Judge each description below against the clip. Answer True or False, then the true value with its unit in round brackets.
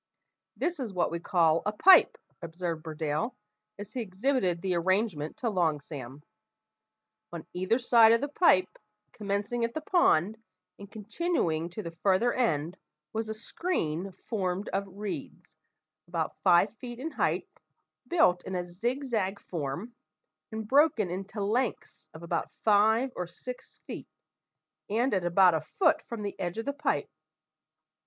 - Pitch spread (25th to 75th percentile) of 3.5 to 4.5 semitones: False (5.3 semitones)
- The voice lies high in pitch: True (200 Hz)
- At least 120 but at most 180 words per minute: True (150 wpm)